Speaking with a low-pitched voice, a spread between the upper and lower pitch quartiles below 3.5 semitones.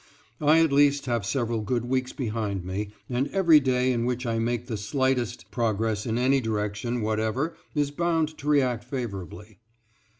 No: low, 120 Hz; average, 3.9 semitones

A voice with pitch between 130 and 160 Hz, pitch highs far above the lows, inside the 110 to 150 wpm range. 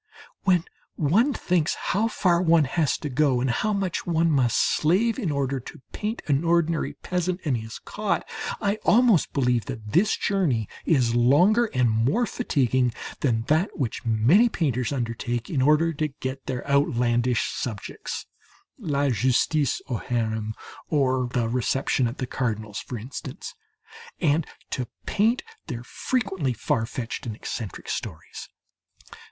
Yes: medium, 140 Hz; wide, 6.1 semitones; average, 145 wpm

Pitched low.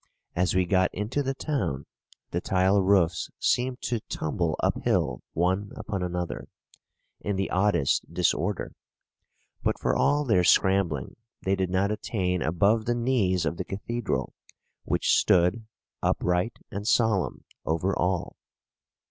Yes: very low, 95 Hz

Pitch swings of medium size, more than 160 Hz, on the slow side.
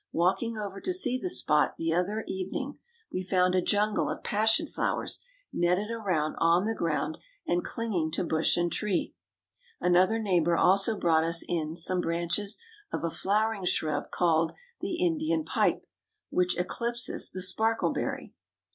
No: average, 4.5 semitones; medium, 185 Hz; average, 150 wpm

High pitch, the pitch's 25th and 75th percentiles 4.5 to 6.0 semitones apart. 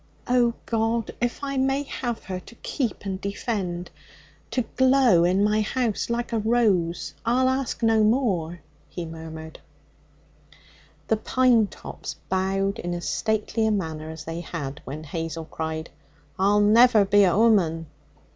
Yes: high, 205 Hz; wide, 5.6 semitones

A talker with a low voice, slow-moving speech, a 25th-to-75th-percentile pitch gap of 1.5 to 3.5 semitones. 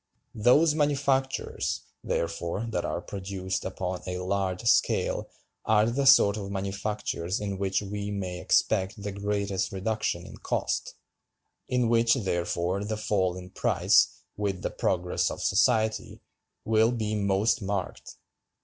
Yes: low, 100 Hz; slow, 130 wpm; average, 2.7 semitones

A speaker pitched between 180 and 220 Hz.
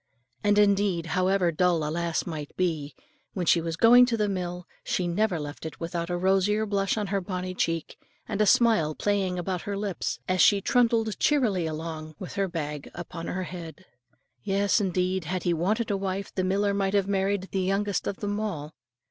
Yes: medium, 185 Hz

